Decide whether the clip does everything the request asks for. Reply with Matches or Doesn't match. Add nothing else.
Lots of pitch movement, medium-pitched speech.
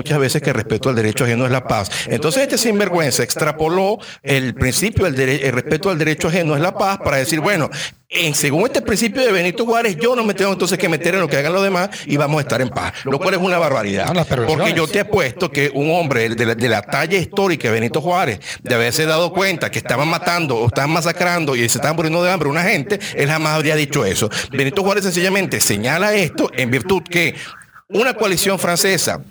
Matches